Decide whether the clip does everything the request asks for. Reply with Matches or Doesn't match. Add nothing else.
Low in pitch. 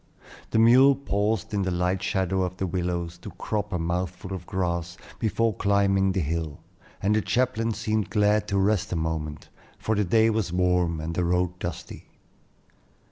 Matches